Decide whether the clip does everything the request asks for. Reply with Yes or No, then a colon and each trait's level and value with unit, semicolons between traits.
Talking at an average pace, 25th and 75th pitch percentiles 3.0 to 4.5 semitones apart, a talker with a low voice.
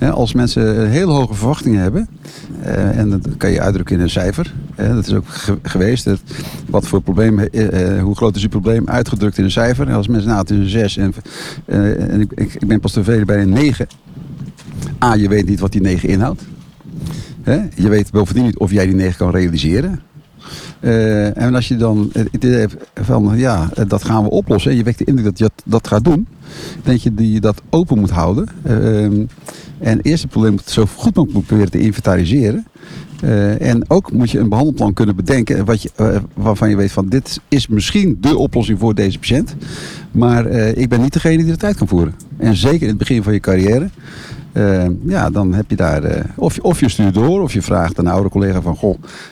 No: fast, 220 wpm; average, 3.7 semitones; low, 110 Hz